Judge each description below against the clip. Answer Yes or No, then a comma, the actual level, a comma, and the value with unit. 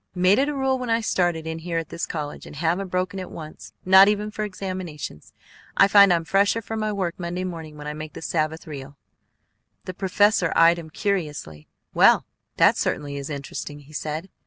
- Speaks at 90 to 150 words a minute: No, average, 200 wpm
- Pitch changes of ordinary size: Yes, average, 4.2 semitones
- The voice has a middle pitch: Yes, medium, 175 Hz